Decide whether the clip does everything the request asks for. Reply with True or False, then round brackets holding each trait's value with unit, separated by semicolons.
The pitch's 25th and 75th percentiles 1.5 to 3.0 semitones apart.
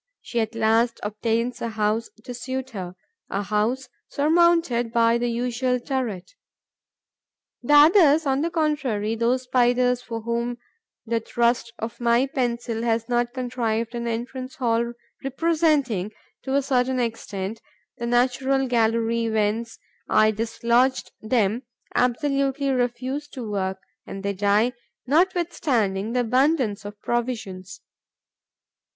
True (2.7 semitones)